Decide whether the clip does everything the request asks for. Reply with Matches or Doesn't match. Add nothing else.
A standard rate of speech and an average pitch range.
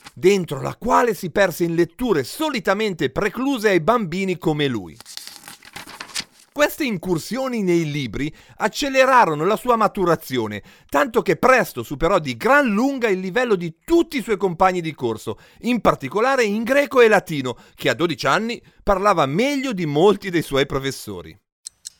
Doesn't match